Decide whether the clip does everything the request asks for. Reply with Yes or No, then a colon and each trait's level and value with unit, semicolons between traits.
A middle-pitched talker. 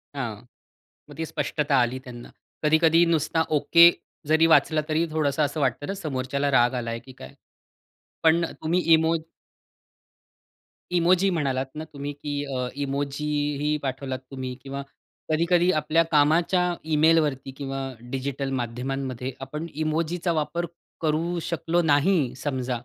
Yes: medium, 145 Hz